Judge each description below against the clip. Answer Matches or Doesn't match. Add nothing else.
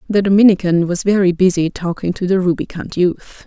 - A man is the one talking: Doesn't match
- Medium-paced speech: Matches